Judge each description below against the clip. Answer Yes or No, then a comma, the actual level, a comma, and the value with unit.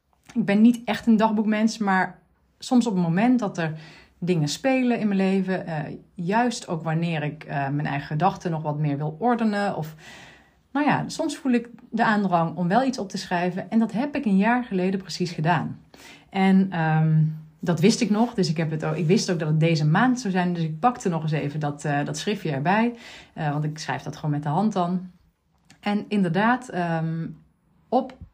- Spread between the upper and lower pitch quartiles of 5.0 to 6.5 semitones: Yes, wide, 5.6 semitones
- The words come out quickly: Yes, fast, 210 wpm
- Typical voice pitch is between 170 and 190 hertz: Yes, medium, 185 Hz